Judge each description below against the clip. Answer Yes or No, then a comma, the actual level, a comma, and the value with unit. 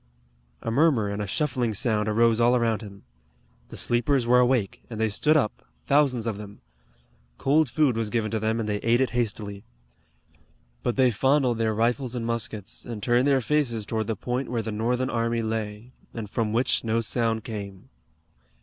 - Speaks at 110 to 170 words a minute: No, average, 185 wpm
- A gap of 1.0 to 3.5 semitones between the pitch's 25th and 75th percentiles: Yes, narrow, 2.5 semitones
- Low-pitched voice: Yes, low, 115 Hz